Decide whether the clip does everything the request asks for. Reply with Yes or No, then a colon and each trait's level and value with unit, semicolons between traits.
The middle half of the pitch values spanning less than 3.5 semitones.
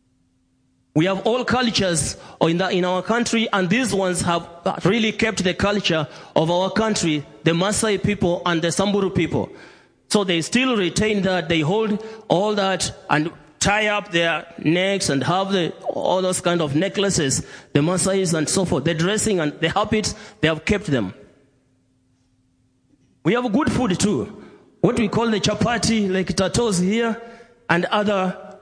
No: average, 4.5 semitones